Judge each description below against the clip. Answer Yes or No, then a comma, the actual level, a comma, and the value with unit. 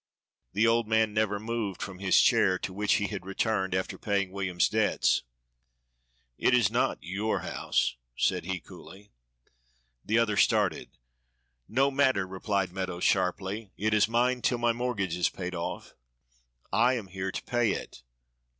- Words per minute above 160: No, average, 155 wpm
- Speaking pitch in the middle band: No, low, 100 Hz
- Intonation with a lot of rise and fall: No, average, 3.2 semitones